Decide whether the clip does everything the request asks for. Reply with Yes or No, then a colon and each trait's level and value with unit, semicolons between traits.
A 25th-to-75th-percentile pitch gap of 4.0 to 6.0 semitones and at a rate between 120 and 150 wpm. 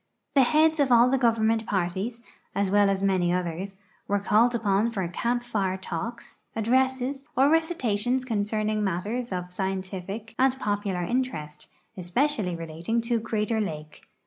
Yes: average, 4.3 semitones; average, 145 wpm